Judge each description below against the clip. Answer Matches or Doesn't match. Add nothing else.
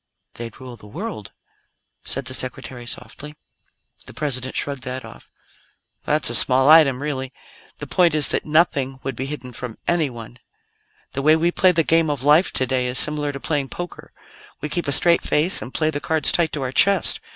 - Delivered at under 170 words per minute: Doesn't match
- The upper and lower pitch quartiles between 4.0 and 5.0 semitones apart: Doesn't match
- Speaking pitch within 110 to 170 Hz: Matches